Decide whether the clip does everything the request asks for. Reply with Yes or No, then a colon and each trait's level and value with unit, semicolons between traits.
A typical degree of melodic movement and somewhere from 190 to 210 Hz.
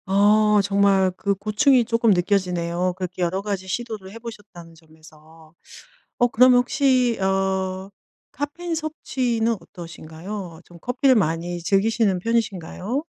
Yes: average, 4.5 semitones; high, 200 Hz